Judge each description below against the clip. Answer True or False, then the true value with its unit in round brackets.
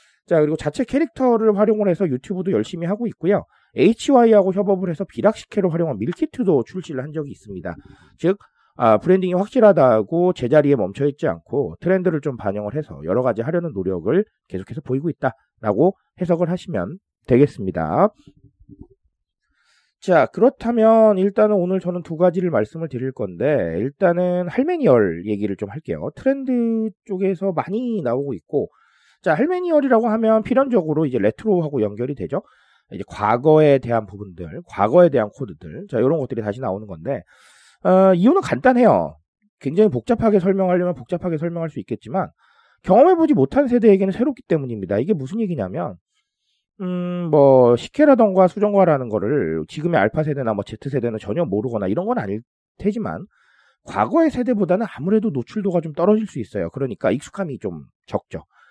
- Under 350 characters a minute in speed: False (375 characters per minute)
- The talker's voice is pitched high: False (180 Hz)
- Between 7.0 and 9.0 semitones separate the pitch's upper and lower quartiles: True (8.5 semitones)